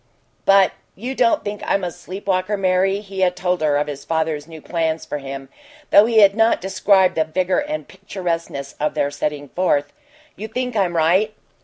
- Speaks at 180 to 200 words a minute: Yes, average, 190 wpm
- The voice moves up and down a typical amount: Yes, average, 4.1 semitones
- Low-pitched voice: No, medium, 185 Hz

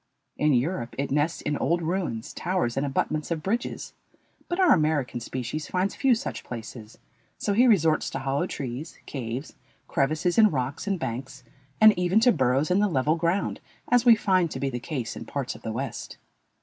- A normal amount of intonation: No, wide, 6.0 semitones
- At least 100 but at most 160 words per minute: No, average, 190 wpm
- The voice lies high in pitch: No, medium, 155 Hz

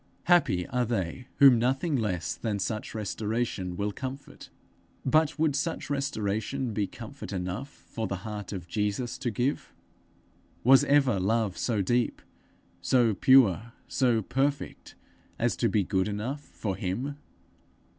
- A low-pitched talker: Yes, low, 115 Hz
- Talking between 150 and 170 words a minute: No, average, 140 wpm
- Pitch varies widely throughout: No, average, 4.8 semitones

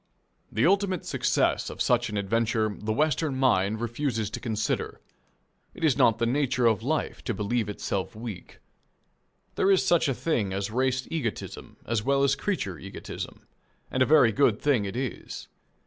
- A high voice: No, low, 120 Hz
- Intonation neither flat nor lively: Yes, average, 4.5 semitones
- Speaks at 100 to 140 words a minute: No, average, 165 wpm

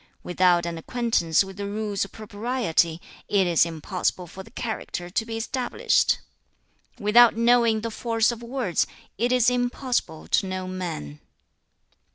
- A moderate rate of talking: Yes, average, 155 wpm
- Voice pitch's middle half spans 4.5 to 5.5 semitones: Yes, average, 4.9 semitones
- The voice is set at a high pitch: Yes, high, 210 Hz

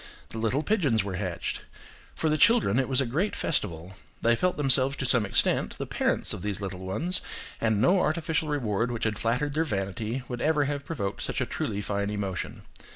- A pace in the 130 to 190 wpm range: No, average, 200 wpm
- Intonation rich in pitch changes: Yes, wide, 6.5 semitones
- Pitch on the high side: No, low, 120 Hz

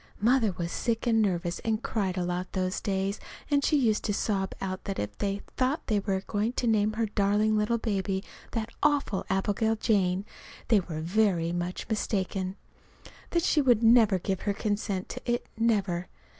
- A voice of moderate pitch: No, high, 205 Hz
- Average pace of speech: Yes, average, 180 wpm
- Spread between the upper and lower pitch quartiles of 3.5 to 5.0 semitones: No, average, 2.9 semitones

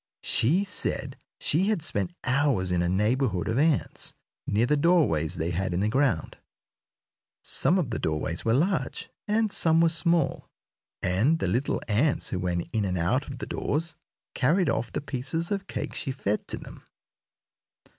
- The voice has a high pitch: No, low, 130 Hz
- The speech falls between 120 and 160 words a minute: No, average, 170 wpm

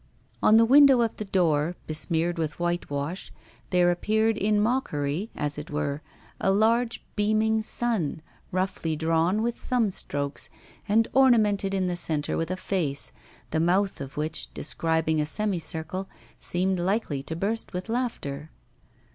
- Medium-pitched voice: Yes, medium, 180 Hz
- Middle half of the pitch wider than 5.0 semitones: Yes, wide, 5.4 semitones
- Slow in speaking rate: No, average, 145 wpm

